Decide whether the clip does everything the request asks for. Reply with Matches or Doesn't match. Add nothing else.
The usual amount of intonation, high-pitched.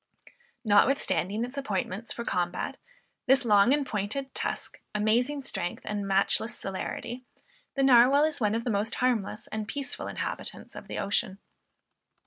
Matches